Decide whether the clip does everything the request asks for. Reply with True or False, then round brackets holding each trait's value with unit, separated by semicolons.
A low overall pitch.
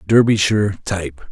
True (100 Hz)